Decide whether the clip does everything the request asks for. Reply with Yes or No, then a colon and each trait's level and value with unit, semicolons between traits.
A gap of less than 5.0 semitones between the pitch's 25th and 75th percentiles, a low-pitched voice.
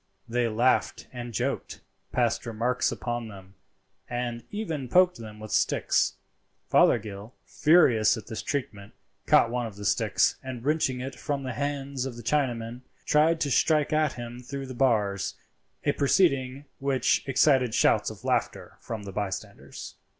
Yes: average, 3.6 semitones; low, 125 Hz